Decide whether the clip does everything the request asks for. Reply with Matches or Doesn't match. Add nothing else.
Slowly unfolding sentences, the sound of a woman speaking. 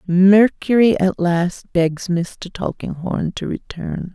Matches